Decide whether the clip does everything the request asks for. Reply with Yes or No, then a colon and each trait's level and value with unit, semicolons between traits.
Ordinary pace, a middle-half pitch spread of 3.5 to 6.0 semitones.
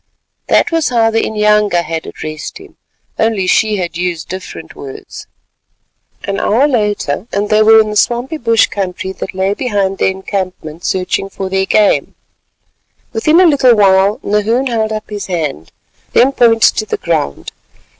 No: average, 155 wpm; average, 3.1 semitones